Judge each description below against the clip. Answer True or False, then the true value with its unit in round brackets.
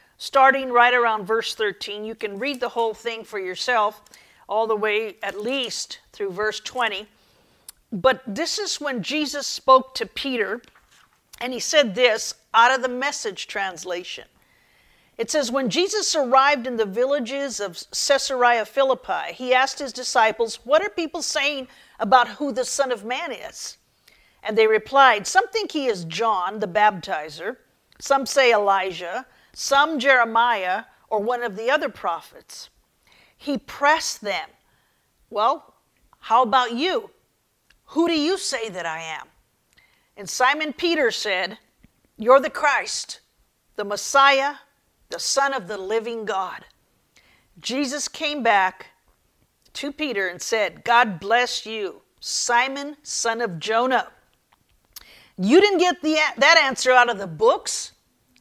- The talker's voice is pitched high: True (250 Hz)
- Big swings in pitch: False (4.5 semitones)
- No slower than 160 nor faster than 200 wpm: False (140 wpm)